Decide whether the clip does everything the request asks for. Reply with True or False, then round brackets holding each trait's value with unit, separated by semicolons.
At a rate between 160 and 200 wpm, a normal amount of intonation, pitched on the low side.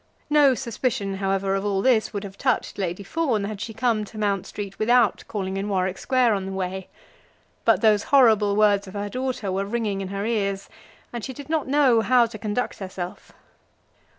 False (195 wpm; 3.5 semitones; 210 Hz)